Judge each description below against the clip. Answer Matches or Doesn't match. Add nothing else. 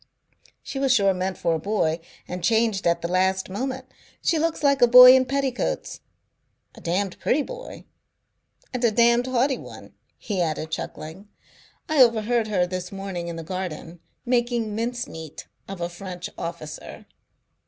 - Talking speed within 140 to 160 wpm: Matches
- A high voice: Matches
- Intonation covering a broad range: Matches